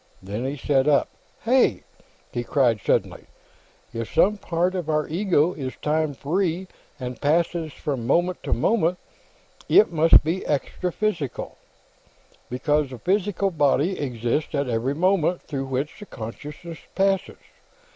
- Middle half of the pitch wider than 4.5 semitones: Yes, average, 5.1 semitones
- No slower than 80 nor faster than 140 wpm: Yes, slow, 135 wpm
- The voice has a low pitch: No, medium, 155 Hz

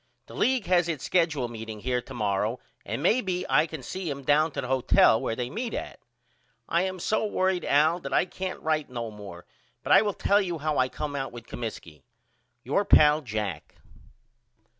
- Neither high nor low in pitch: Yes, medium, 150 Hz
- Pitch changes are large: Yes, wide, 6.9 semitones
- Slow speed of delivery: No, average, 200 wpm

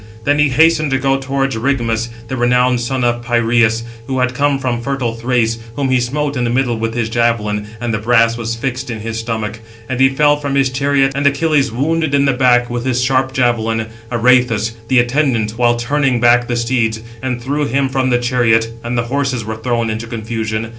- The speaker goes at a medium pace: No, fast, 210 wpm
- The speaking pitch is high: No, low, 120 Hz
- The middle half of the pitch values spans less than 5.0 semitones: Yes, average, 2.7 semitones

